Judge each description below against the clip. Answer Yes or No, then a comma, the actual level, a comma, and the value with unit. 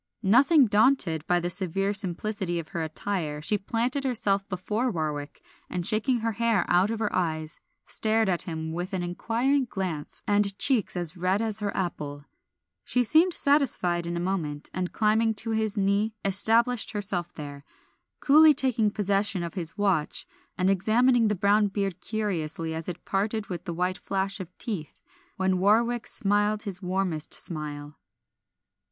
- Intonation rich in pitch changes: No, average, 4.1 semitones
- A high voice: Yes, high, 195 Hz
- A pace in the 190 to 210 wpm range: No, average, 160 wpm